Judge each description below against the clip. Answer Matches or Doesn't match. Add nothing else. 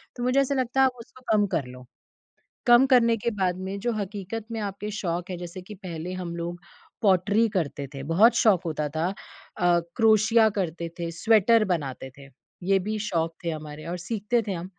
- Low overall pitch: Doesn't match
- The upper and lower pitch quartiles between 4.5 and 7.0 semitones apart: Matches